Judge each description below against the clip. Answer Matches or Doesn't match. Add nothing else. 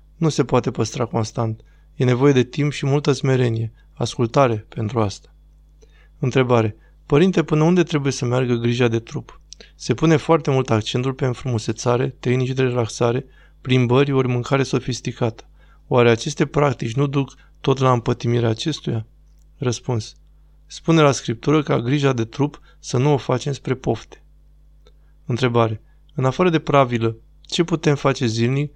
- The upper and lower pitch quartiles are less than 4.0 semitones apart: Matches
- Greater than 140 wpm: Matches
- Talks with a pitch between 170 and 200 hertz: Doesn't match